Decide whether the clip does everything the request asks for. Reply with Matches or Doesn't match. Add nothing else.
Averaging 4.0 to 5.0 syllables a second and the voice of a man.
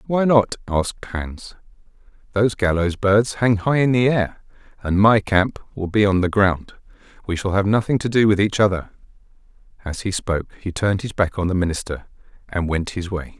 Doesn't match